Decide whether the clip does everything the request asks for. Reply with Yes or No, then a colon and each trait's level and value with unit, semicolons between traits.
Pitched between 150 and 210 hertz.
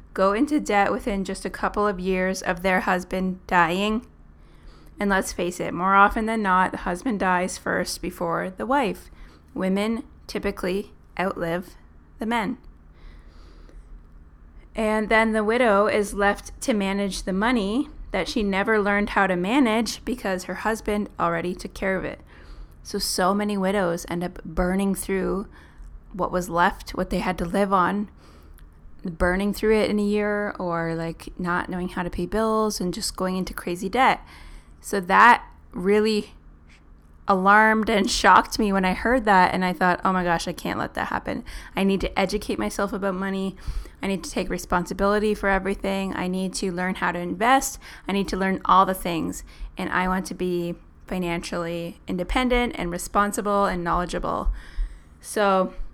Yes: high, 190 Hz